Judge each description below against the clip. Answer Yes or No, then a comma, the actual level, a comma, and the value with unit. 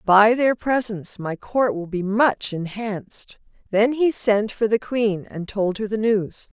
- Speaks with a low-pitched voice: No, high, 215 Hz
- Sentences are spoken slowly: No, average, 180 wpm